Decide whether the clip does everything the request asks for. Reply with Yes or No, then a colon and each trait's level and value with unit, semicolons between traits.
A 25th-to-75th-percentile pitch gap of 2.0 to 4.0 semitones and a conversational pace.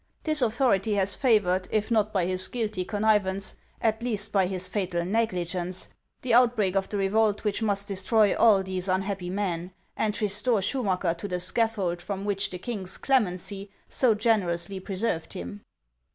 Yes: average, 2.9 semitones; average, 160 wpm